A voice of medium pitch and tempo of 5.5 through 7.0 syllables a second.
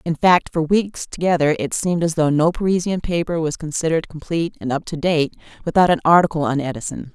Yes: medium, 160 Hz; 6.0 syllables/s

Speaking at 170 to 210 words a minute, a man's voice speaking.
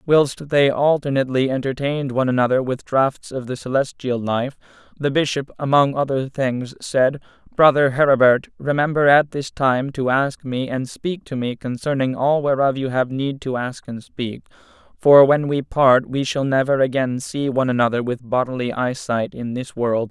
Yes: average, 175 wpm; male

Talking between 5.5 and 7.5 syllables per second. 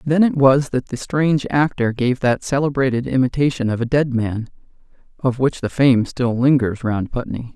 No: 4.9 syllables/s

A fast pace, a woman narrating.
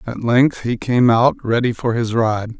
No: fast, 210 wpm; male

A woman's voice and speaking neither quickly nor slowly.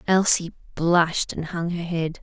Yes: female; average, 160 wpm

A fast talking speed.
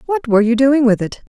Yes: fast, 275 wpm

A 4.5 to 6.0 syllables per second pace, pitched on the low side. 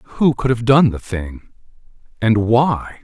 No: 3.5 syllables/s; low, 115 Hz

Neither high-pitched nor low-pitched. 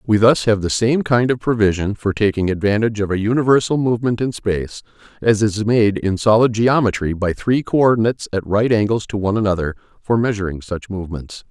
No: low, 105 Hz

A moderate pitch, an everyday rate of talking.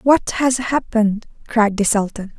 No: high, 225 Hz; average, 150 wpm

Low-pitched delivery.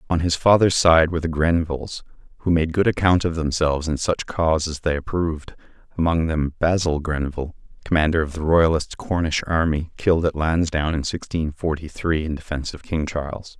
Yes: very low, 80 Hz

